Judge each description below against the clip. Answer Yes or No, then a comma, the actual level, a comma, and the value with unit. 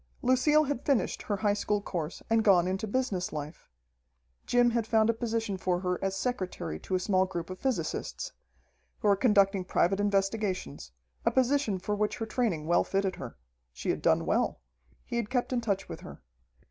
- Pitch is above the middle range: Yes, high, 205 Hz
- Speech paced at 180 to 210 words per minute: Yes, average, 185 wpm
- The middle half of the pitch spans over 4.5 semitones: No, average, 4.0 semitones